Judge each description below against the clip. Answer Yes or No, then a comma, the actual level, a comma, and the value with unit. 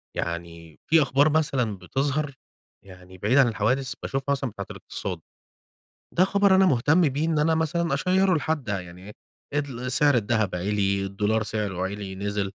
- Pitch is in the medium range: No, low, 120 Hz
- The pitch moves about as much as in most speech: No, wide, 7.1 semitones